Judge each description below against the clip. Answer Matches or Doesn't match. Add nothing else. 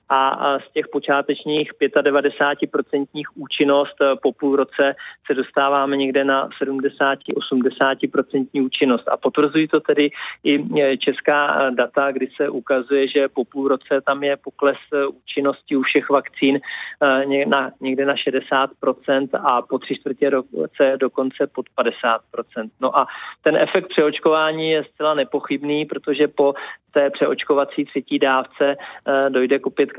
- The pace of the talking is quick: Doesn't match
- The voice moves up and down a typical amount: Doesn't match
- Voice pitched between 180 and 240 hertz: Doesn't match